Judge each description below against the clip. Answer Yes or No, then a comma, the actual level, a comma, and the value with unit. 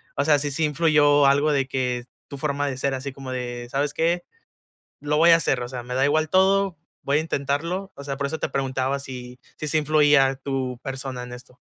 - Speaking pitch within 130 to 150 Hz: Yes, medium, 140 Hz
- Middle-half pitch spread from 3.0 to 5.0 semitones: No, narrow, 2.5 semitones